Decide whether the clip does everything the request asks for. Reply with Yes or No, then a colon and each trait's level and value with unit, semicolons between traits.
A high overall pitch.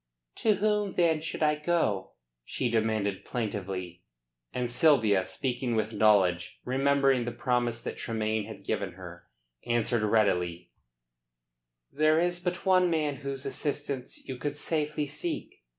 No: low, 125 Hz